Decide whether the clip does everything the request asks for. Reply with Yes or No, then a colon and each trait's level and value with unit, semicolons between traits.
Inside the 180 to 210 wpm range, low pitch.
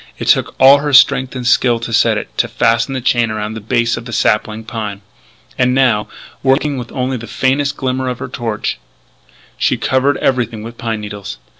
Yes: average, 195 wpm; low, 120 Hz